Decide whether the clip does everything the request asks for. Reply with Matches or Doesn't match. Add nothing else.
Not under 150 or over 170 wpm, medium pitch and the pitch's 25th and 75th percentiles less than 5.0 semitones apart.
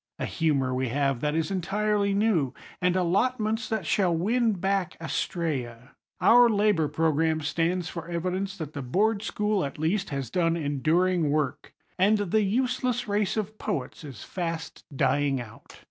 Doesn't match